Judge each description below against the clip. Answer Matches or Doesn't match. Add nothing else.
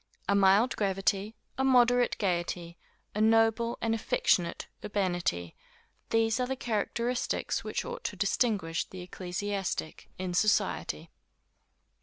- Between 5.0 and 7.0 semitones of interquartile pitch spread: Doesn't match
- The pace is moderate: Doesn't match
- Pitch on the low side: Doesn't match